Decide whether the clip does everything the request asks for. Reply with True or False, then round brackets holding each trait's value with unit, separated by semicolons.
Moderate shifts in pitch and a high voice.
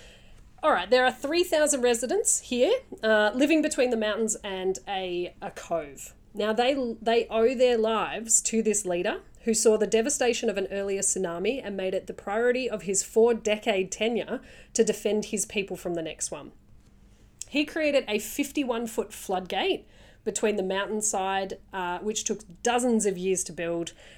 True (3.8 semitones; 215 Hz)